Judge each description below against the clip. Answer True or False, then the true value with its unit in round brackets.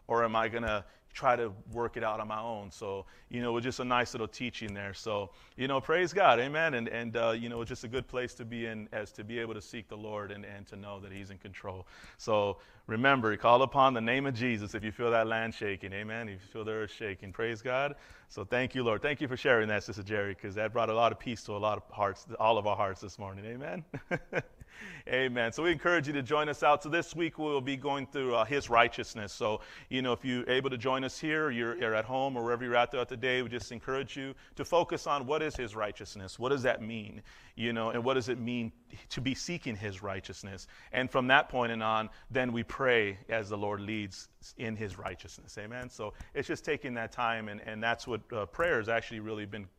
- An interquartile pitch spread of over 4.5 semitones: False (3.4 semitones)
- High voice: False (115 Hz)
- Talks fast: True (255 wpm)